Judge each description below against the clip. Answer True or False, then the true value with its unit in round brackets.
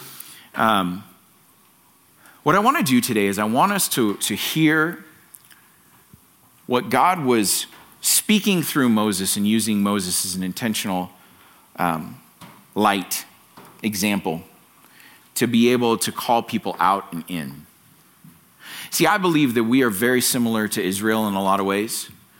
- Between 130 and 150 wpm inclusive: True (140 wpm)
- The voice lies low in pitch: True (110 Hz)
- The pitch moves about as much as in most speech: True (3.9 semitones)